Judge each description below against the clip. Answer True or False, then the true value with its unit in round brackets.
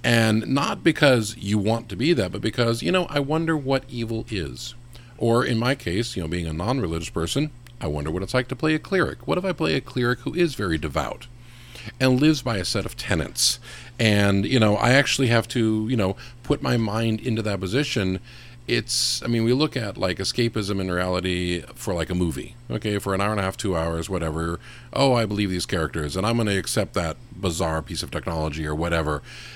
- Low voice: True (115 Hz)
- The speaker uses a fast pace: True (225 wpm)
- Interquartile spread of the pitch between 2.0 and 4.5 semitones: False (5.0 semitones)